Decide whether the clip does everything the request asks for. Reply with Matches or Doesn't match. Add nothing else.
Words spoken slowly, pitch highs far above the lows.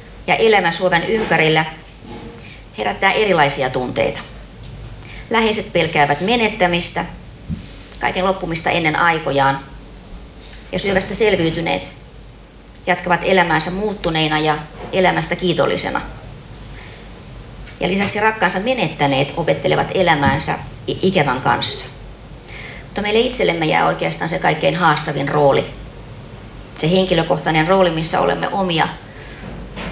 Matches